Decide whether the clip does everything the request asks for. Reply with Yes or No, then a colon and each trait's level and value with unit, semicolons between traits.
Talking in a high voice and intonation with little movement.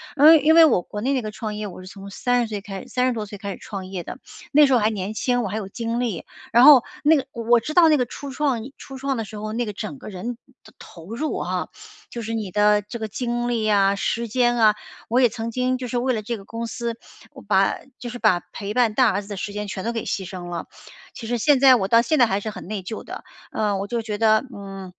No: high, 225 Hz; average, 3.2 semitones